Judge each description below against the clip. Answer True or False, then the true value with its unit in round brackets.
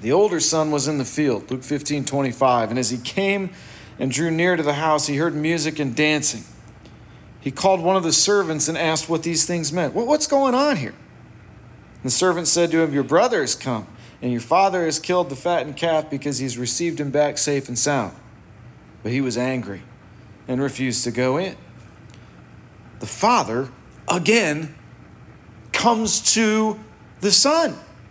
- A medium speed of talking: True (180 wpm)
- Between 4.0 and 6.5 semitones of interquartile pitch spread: True (5.6 semitones)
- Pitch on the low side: False (150 Hz)